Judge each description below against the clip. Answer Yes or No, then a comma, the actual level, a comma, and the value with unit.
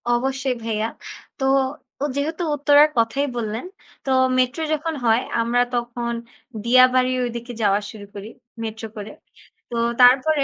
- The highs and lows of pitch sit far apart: No, average, 3.2 semitones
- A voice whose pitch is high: Yes, high, 245 Hz